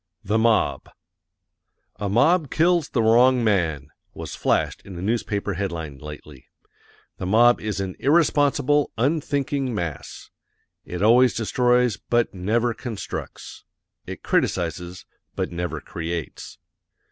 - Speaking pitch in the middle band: No, low, 110 Hz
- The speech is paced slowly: Yes, slow, 115 wpm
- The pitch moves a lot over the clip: Yes, wide, 6.1 semitones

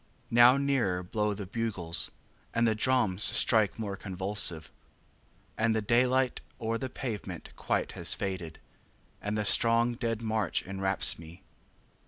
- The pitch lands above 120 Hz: No, low, 110 Hz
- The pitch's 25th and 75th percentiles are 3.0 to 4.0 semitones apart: Yes, average, 3.5 semitones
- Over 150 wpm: No, average, 140 wpm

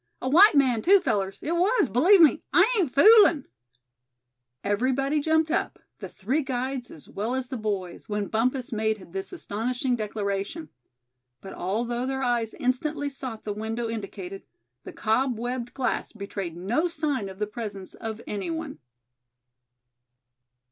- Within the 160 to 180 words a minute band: No, average, 150 wpm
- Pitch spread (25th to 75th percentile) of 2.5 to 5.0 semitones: No, wide, 5.4 semitones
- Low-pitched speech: No, high, 245 Hz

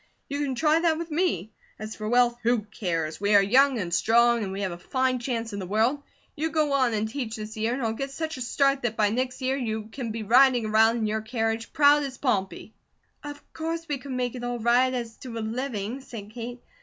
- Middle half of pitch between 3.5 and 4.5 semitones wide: Yes, average, 3.8 semitones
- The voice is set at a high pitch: Yes, high, 240 Hz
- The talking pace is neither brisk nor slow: No, fast, 240 wpm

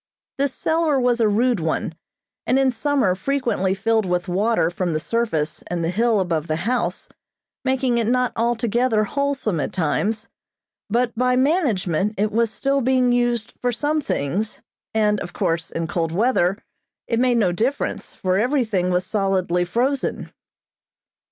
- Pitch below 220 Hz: No, high, 225 Hz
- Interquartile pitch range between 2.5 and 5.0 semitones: No, wide, 5.5 semitones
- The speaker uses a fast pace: No, average, 155 wpm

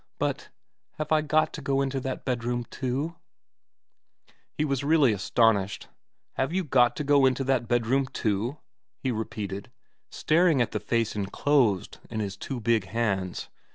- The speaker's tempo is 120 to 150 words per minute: No, average, 165 wpm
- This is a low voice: Yes, low, 125 Hz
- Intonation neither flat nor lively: Yes, average, 4.2 semitones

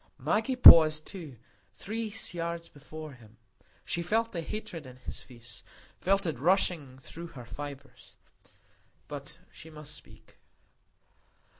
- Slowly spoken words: Yes, slow, 125 wpm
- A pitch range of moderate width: Yes, average, 4.7 semitones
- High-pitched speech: No, medium, 155 Hz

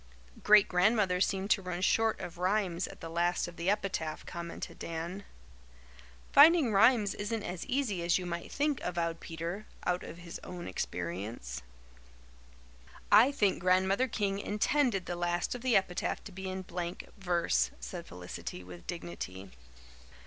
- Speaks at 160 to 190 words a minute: No, average, 150 wpm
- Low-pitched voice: No, medium, 180 Hz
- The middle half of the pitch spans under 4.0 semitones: Yes, average, 3.4 semitones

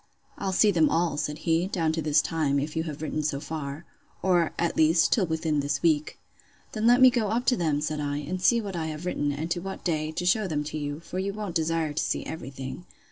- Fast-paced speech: Yes, fast, 245 wpm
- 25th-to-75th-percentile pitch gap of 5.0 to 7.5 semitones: No, average, 3.3 semitones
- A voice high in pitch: No, medium, 160 Hz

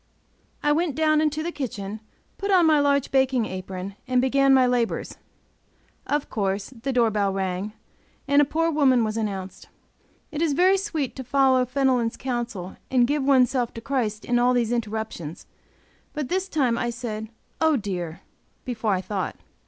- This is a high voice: Yes, very high, 250 Hz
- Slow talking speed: No, average, 170 wpm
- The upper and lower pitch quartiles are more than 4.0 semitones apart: Yes, average, 4.8 semitones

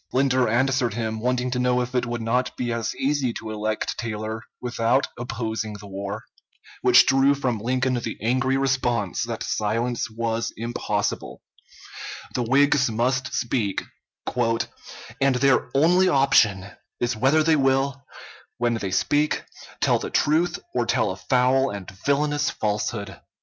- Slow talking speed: No, average, 145 wpm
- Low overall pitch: Yes, low, 120 Hz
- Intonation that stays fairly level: No, average, 3.3 semitones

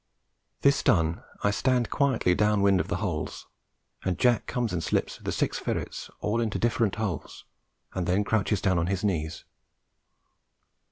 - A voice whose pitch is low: Yes, low, 100 Hz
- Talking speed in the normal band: Yes, average, 160 wpm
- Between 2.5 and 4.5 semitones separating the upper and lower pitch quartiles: Yes, average, 4.0 semitones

